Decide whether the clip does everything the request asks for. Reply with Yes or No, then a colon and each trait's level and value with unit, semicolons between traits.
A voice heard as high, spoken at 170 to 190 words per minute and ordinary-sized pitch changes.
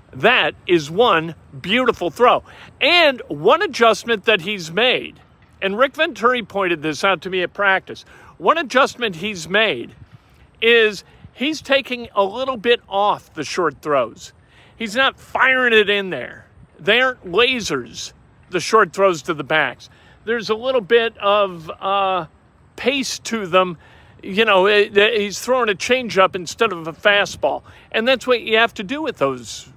No: high, 210 Hz; average, 155 wpm; average, 4.7 semitones